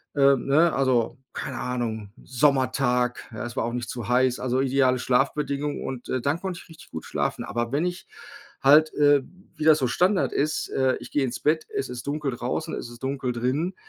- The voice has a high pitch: No, low, 135 Hz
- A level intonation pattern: No, average, 3.2 semitones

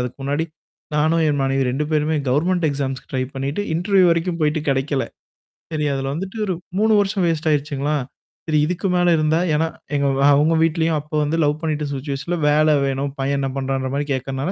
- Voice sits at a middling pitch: Yes, medium, 150 Hz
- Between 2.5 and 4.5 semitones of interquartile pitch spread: Yes, average, 3.1 semitones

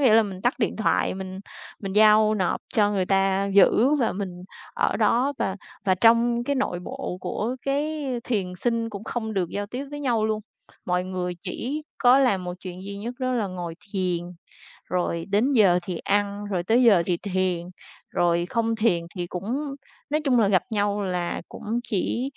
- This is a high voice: Yes, high, 205 Hz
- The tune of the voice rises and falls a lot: No, average, 4.4 semitones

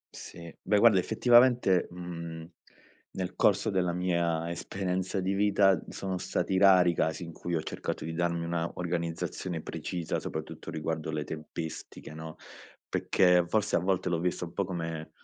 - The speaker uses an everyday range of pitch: No, narrow, 2.3 semitones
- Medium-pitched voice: No, very low, 90 Hz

